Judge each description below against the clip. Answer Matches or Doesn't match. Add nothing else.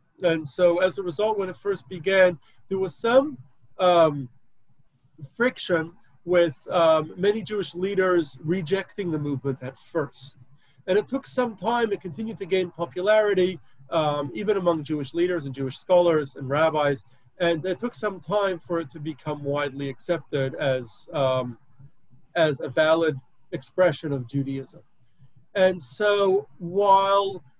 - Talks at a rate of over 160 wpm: Doesn't match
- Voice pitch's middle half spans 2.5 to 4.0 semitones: Doesn't match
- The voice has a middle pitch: Matches